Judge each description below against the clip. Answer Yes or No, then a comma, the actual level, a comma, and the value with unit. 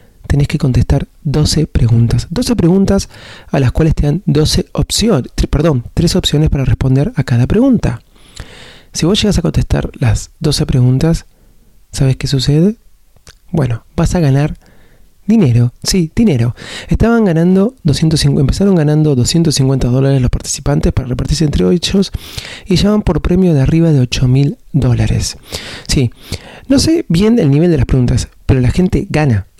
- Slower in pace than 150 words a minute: No, average, 155 wpm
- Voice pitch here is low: No, medium, 145 Hz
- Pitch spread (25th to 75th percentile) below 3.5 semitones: No, wide, 5.5 semitones